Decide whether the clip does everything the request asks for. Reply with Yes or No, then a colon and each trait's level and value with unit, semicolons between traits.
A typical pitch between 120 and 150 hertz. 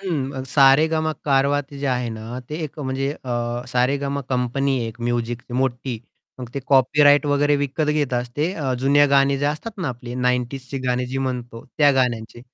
Yes: low, 135 Hz